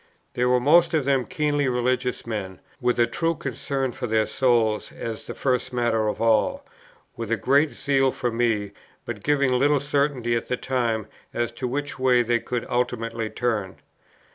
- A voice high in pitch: No, low, 125 Hz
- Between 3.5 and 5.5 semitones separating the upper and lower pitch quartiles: No, average, 2.8 semitones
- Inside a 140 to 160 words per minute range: No, average, 175 wpm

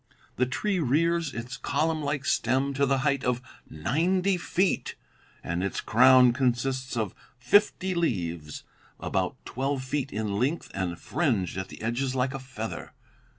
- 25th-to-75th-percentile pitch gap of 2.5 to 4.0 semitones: No, average, 4.4 semitones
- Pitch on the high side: No, low, 130 Hz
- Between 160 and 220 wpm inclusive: No, average, 150 wpm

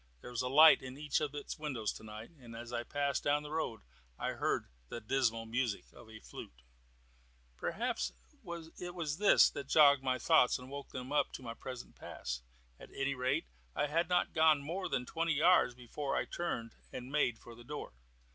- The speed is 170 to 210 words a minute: Yes, average, 195 wpm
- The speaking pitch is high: No, low, 135 Hz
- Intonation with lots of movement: No, average, 4.1 semitones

